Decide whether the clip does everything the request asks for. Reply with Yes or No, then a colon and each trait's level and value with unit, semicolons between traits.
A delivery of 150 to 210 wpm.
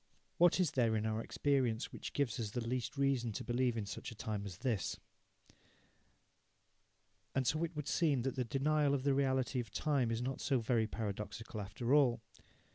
Yes: average, 190 wpm